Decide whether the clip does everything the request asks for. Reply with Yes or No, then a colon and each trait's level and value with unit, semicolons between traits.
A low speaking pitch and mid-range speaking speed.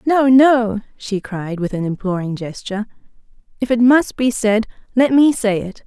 No: high, 225 Hz; average, 175 wpm